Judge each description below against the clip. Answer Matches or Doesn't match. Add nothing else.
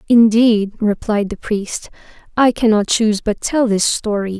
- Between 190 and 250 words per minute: Doesn't match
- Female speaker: Matches